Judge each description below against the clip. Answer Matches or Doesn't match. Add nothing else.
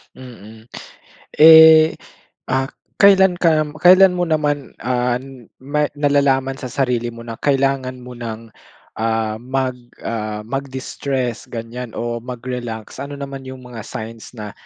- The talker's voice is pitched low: Matches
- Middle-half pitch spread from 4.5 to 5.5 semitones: Doesn't match